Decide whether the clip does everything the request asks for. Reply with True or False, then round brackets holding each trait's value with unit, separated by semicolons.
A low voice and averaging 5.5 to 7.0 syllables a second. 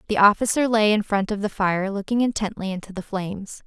False (205 Hz; 5.8 syllables/s)